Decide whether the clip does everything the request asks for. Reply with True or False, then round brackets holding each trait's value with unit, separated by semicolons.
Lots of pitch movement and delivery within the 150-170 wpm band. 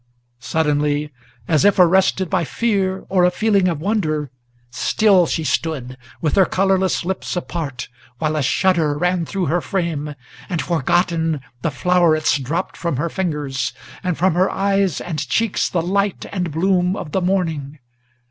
False (3.8 semitones; 155 wpm)